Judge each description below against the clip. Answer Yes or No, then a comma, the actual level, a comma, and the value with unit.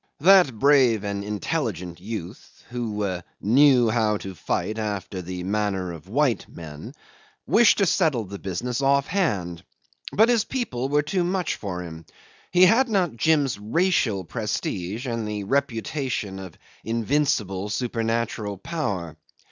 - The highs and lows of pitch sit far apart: Yes, wide, 6.9 semitones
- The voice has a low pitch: Yes, low, 115 Hz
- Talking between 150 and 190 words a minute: No, slow, 135 wpm